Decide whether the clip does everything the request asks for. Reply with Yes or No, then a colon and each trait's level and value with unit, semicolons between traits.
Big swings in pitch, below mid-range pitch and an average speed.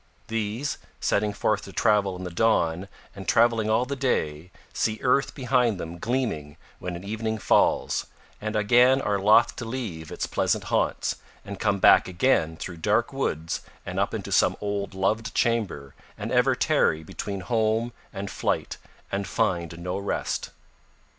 No: average, 4.1 semitones; low, 105 Hz; average, 155 wpm